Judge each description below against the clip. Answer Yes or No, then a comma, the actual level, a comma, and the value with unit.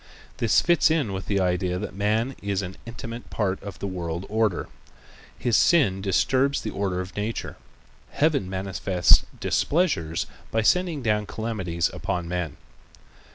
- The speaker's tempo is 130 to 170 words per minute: Yes, average, 145 wpm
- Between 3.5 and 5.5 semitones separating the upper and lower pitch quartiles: Yes, average, 4.1 semitones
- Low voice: Yes, low, 100 Hz